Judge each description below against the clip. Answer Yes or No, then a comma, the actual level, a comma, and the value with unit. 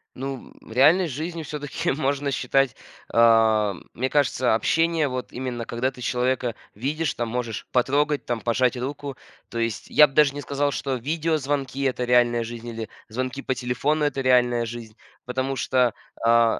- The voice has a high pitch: No, low, 130 Hz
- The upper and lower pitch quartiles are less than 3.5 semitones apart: Yes, average, 3.0 semitones